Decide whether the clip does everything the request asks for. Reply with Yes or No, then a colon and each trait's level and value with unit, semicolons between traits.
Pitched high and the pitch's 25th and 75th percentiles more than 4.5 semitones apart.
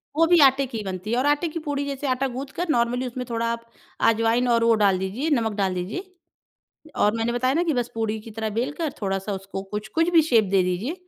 Yes: high, 235 Hz; average, 4.9 semitones